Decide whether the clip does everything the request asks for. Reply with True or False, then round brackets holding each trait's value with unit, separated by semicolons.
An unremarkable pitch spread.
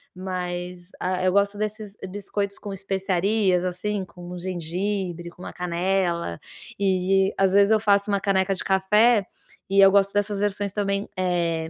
False (1.9 semitones)